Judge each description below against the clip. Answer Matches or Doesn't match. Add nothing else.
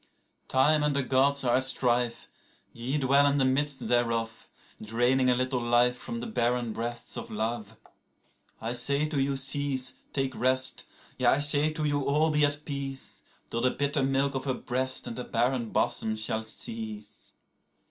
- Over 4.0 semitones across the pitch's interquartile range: Doesn't match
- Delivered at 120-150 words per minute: Doesn't match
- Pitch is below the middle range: Matches